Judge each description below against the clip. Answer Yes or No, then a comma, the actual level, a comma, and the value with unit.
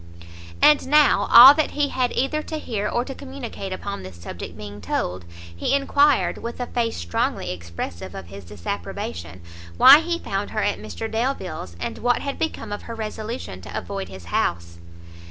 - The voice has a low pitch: No, high, 210 Hz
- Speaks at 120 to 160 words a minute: No, average, 175 wpm